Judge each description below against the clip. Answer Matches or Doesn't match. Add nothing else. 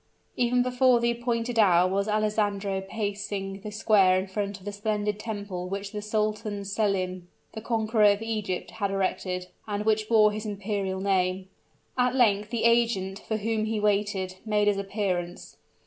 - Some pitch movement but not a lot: Doesn't match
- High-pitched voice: Matches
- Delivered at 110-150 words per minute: Doesn't match